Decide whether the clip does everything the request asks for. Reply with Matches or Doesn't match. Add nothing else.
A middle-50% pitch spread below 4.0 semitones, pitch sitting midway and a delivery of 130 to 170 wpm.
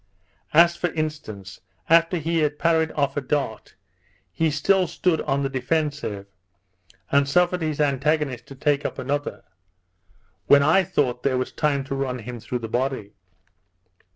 Matches